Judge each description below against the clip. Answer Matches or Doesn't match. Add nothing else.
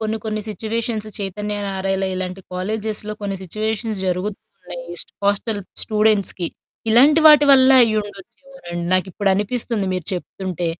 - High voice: Matches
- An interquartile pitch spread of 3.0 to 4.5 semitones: Doesn't match